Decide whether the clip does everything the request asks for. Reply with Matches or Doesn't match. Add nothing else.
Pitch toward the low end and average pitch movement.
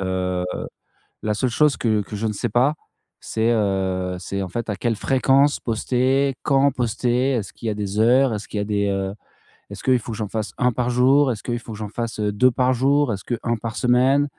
Matches